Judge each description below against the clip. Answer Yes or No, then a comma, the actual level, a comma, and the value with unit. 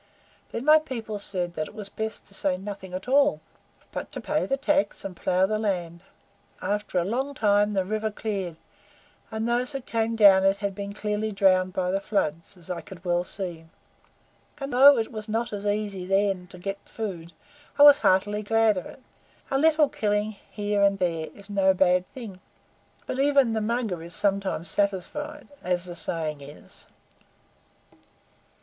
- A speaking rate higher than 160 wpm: Yes, average, 180 wpm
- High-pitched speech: Yes, high, 205 Hz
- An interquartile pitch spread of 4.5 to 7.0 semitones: No, average, 3.4 semitones